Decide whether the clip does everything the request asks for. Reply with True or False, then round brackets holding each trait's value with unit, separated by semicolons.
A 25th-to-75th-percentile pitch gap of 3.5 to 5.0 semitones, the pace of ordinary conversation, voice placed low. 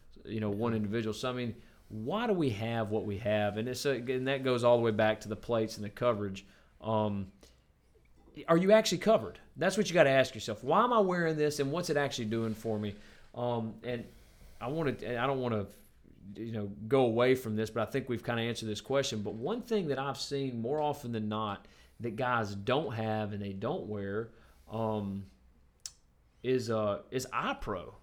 False (3.9 semitones; 215 wpm; 115 Hz)